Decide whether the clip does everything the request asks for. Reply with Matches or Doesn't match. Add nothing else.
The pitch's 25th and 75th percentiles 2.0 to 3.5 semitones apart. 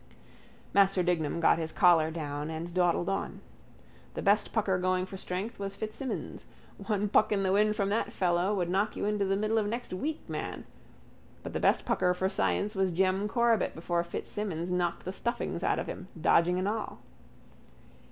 Matches